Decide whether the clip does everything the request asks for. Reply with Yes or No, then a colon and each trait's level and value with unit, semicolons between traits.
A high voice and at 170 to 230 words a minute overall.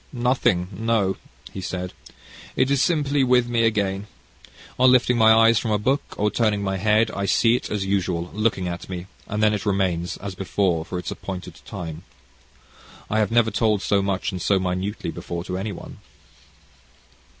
No: low, 100 Hz; average, 180 wpm